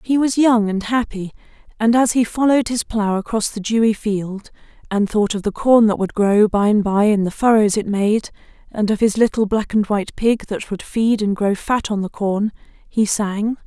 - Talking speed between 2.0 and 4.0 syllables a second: No, 4.9 syllables/s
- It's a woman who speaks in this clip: Yes, female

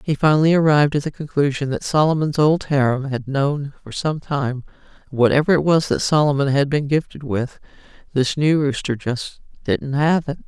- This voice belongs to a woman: Yes, female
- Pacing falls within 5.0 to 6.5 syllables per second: Yes, 5.1 syllables/s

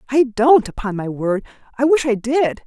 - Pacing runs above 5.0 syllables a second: No, 4.7 syllables/s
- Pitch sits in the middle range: No, high, 245 Hz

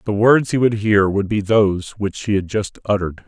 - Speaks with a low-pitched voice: Yes, low, 105 Hz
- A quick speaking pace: Yes, fast, 240 wpm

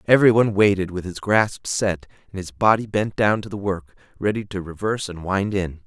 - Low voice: Yes, low, 100 Hz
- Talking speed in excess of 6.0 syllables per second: No, 5.5 syllables/s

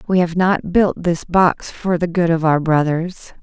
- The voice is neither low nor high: Yes, medium, 170 Hz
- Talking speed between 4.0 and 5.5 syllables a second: Yes, 4.1 syllables/s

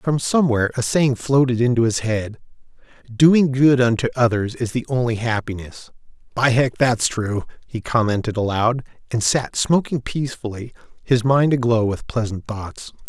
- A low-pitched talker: Yes, low, 120 Hz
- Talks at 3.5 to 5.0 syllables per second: Yes, 4.8 syllables/s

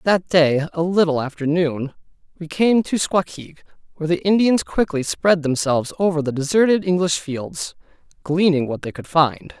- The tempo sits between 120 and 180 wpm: Yes, average, 165 wpm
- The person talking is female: No, male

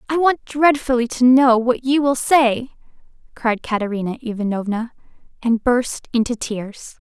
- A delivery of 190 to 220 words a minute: No, slow, 135 wpm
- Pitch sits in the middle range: No, high, 245 Hz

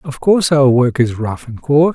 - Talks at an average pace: No, fast, 245 wpm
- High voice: No, low, 135 Hz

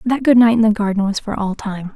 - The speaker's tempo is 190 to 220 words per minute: No, fast, 305 wpm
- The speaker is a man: No, female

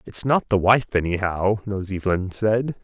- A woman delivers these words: No, male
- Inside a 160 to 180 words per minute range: Yes, average, 170 wpm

